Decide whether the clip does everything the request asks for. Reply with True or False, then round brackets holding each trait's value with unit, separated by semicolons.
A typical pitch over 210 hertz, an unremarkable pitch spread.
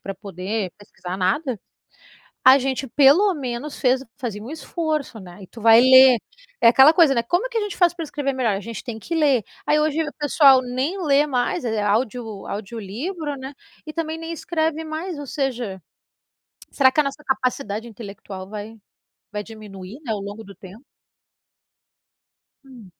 False (255 Hz; 5.8 semitones)